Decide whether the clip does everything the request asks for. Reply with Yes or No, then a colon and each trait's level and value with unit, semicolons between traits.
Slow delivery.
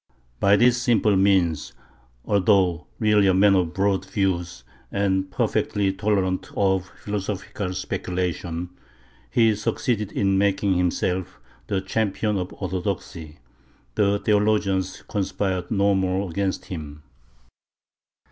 Yes: slow, 110 wpm